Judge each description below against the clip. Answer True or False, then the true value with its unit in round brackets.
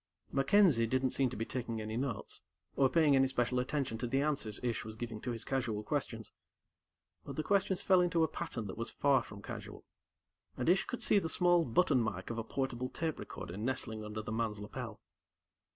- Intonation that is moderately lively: True (4.6 semitones)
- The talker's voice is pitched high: False (125 Hz)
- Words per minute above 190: True (200 wpm)